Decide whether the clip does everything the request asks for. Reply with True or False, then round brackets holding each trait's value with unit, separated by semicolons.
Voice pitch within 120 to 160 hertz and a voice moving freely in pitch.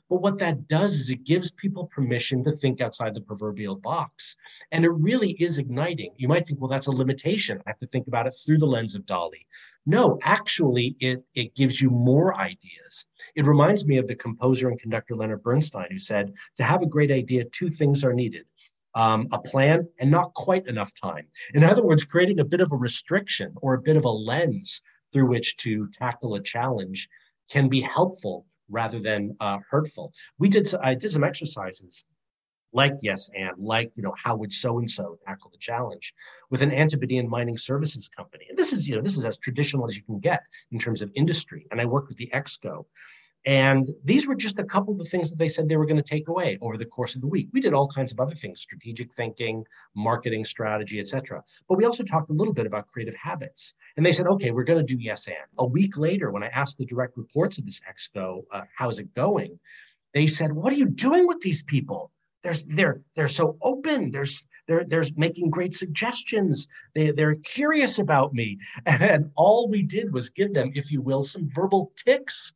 True (140 Hz; 5.9 semitones)